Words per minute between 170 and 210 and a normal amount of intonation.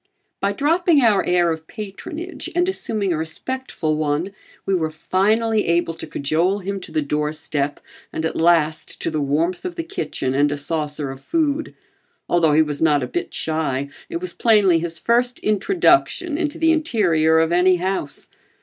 No: average, 175 wpm; wide, 6.9 semitones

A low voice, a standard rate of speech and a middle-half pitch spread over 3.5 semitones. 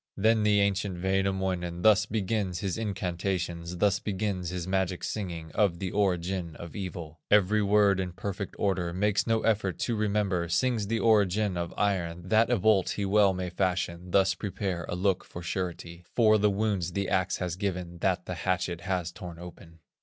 No: very low, 95 Hz; average, 175 wpm; average, 2.7 semitones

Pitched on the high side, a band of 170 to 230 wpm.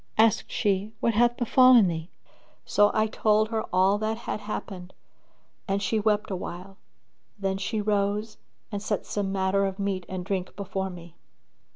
No: high, 200 Hz; average, 160 wpm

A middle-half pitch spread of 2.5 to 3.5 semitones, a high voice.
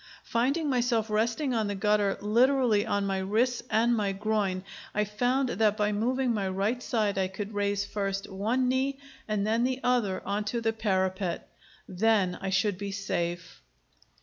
Yes: average, 3.2 semitones; high, 210 Hz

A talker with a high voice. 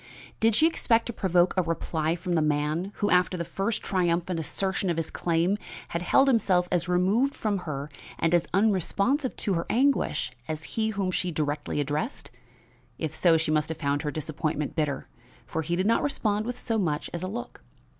No: medium, 180 Hz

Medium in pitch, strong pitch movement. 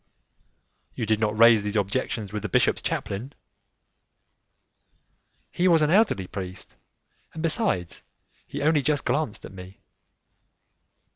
No: low, 110 Hz; wide, 7.4 semitones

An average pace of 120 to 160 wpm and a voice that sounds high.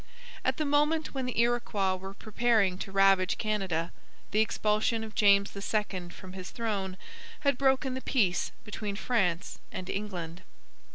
Yes: average, 150 wpm; high, 210 Hz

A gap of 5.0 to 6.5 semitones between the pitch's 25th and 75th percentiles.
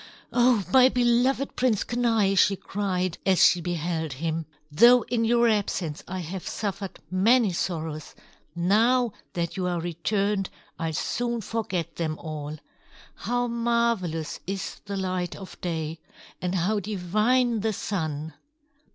Yes: wide, 5.4 semitones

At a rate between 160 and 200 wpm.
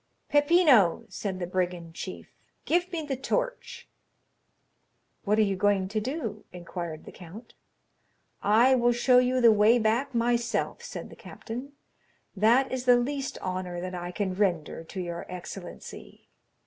No: average, 150 wpm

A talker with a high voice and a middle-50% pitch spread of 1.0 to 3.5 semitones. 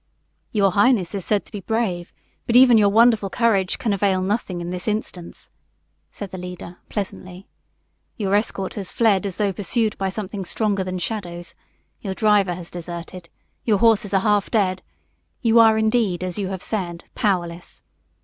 Yes: high, 195 Hz; average, 3.0 semitones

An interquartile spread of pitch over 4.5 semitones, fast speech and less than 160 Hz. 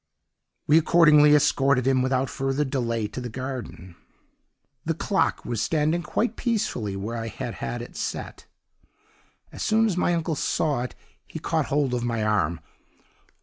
No: average, 5.0 semitones; average, 155 wpm; low, 135 Hz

